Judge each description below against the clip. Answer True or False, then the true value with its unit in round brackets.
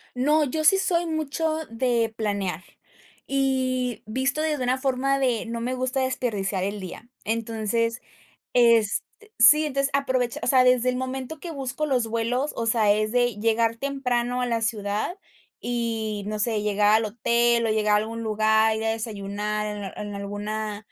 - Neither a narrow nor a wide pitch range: True (3.2 semitones)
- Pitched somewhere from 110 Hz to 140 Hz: False (235 Hz)